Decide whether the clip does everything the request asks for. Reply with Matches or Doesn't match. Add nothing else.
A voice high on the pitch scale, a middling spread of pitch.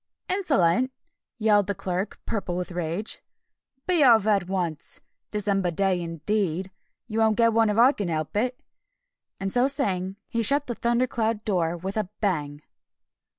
Matches